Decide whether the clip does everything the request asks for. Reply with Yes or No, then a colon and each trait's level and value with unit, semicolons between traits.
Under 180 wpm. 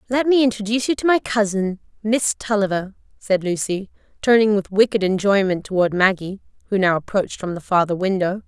Yes: average, 170 wpm